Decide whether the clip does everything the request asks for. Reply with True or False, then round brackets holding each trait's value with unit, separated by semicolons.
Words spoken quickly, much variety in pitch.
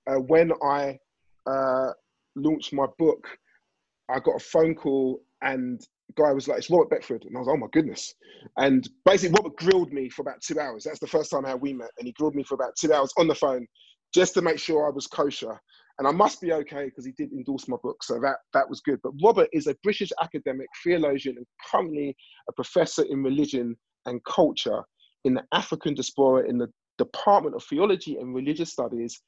True (215 wpm; 7.7 semitones)